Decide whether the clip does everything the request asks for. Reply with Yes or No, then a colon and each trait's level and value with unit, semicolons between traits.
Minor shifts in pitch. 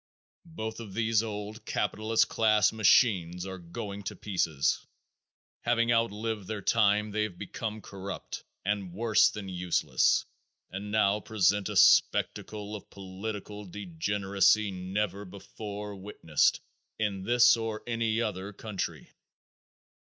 Yes: narrow, 2.2 semitones